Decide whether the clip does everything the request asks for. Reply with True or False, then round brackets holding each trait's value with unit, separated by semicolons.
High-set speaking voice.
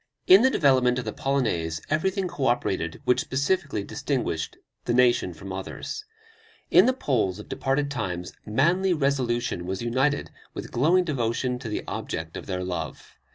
False (125 Hz)